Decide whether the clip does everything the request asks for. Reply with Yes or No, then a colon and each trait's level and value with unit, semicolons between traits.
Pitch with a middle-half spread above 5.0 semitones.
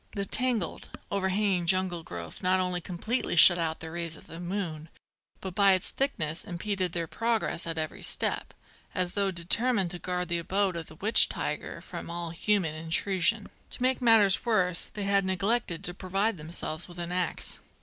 No: average, 2.9 semitones